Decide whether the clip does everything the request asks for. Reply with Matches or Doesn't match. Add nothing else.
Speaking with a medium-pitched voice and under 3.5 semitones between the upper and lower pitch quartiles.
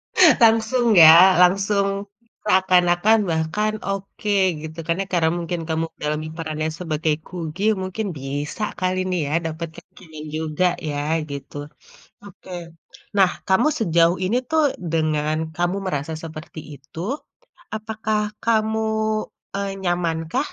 Doesn't match